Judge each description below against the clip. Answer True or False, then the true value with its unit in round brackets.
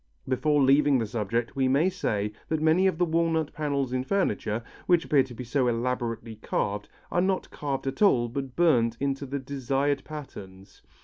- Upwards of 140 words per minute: True (180 wpm)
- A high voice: False (135 Hz)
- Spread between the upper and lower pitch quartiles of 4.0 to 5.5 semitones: True (4.4 semitones)